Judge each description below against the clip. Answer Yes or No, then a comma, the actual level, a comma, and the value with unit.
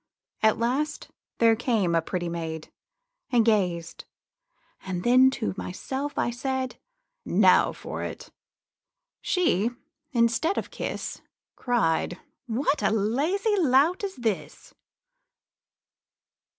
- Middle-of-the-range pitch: No, high, 235 Hz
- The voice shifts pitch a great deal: Yes, wide, 5.7 semitones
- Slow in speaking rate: Yes, slow, 100 wpm